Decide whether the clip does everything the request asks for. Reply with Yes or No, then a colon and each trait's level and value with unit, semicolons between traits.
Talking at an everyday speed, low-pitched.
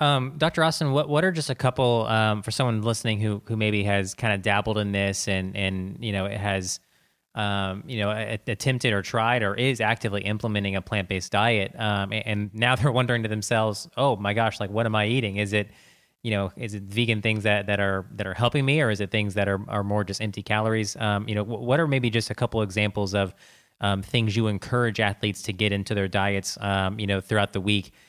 No: fast, 240 wpm; low, 105 Hz